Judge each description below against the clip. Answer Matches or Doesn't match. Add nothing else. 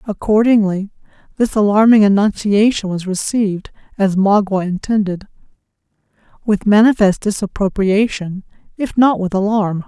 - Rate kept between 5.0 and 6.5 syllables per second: Doesn't match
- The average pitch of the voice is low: Doesn't match